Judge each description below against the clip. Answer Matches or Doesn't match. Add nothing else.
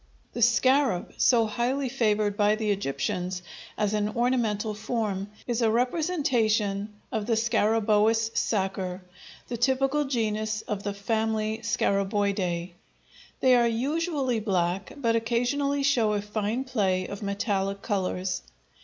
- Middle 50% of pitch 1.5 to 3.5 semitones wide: Matches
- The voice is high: Matches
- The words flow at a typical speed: Doesn't match